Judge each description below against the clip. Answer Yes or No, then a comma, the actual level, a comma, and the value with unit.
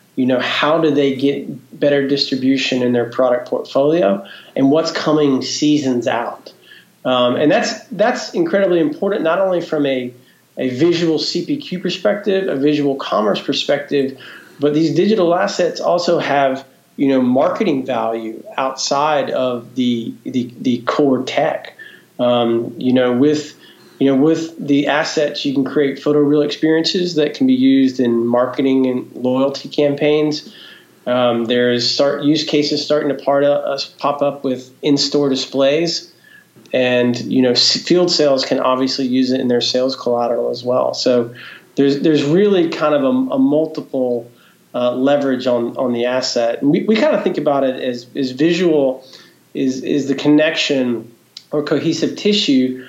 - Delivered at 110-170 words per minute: Yes, average, 160 wpm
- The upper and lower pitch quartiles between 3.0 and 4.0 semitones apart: Yes, average, 3.3 semitones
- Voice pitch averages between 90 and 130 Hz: No, medium, 140 Hz